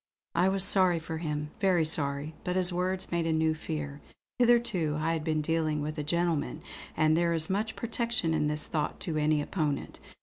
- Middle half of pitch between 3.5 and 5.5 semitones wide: No, average, 2.9 semitones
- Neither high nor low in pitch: Yes, medium, 160 Hz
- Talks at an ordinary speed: Yes, average, 195 wpm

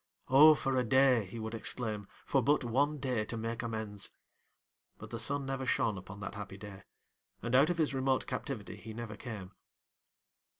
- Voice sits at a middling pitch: No, low, 115 Hz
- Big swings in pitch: No, average, 3.9 semitones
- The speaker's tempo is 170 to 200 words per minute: Yes, average, 180 wpm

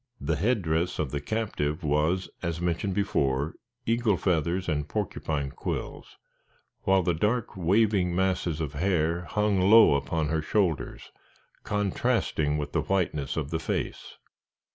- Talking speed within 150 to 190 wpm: No, slow, 135 wpm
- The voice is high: No, very low, 85 Hz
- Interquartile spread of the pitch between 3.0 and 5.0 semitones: Yes, average, 4.3 semitones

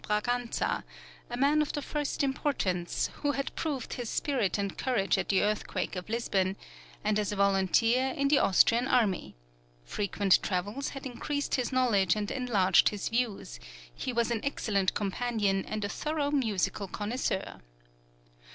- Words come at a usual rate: Yes, average, 150 wpm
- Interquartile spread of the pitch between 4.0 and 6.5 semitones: Yes, average, 4.8 semitones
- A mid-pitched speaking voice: No, high, 225 Hz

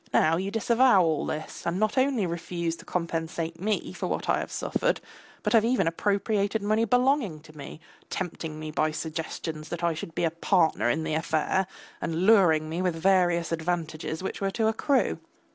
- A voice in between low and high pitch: Yes, medium, 175 Hz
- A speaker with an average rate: Yes, average, 180 wpm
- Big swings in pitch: No, average, 4.2 semitones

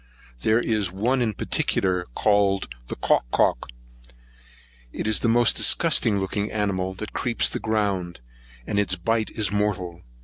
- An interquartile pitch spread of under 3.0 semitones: Yes, narrow, 2.6 semitones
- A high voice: No, low, 105 Hz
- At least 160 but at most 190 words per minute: No, average, 145 wpm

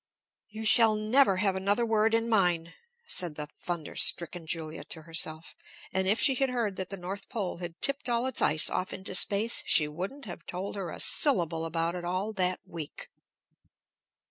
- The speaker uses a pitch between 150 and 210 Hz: Yes, high, 190 Hz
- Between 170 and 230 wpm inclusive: Yes, average, 180 wpm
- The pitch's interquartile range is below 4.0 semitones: No, average, 4.6 semitones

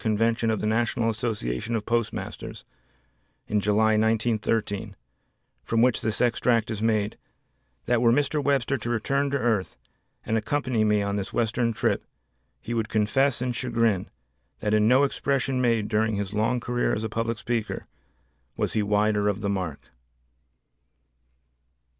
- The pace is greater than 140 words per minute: Yes, average, 150 wpm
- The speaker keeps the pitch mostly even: Yes, narrow, 2.2 semitones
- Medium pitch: No, low, 110 Hz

